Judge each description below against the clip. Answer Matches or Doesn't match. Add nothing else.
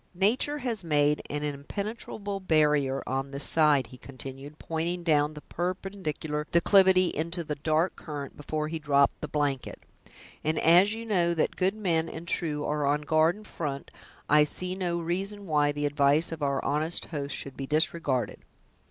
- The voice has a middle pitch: Matches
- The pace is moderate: Matches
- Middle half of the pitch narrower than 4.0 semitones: Matches